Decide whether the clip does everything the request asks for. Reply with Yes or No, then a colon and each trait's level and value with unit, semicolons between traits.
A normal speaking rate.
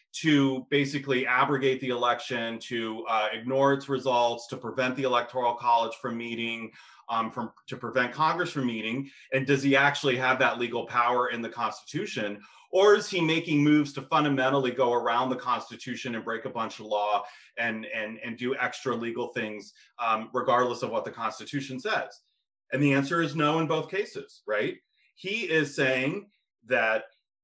Yes: average, 175 wpm